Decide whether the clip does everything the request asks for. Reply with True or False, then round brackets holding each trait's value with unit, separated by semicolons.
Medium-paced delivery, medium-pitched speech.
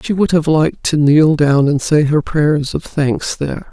False (225 wpm; 150 Hz)